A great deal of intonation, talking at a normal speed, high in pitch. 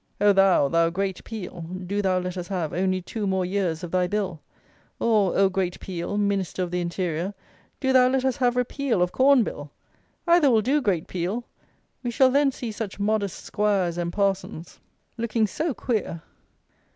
No: average, 4.3 semitones; average, 180 wpm; high, 195 Hz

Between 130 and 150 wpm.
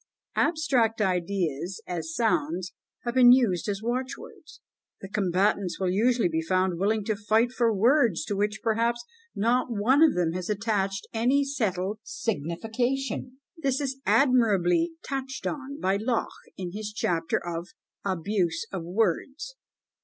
Yes: average, 140 wpm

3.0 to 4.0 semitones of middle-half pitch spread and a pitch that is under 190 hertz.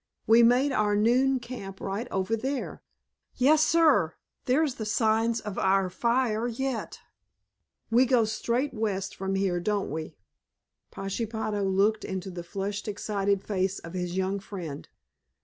No: average, 3.7 semitones; high, 210 Hz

